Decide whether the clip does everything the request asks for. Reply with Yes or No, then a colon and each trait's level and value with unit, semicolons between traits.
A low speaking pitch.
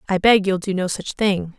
No: high, 190 Hz